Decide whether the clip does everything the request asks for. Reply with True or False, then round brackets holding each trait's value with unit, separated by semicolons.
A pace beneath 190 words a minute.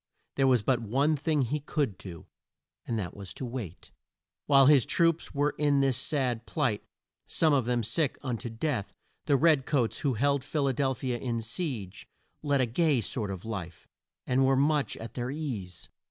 False (195 wpm)